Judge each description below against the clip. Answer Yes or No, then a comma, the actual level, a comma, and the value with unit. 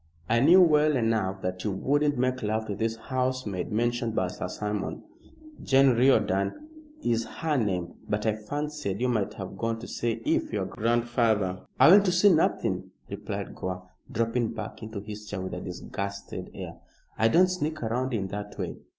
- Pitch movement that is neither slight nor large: Yes, average, 4.4 semitones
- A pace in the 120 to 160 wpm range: No, average, 180 wpm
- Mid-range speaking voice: No, low, 115 Hz